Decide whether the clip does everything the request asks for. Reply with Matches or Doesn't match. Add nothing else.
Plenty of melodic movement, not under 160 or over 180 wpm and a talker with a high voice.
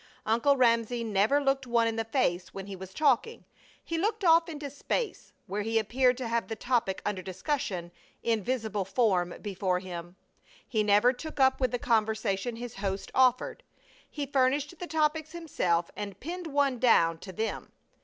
Matches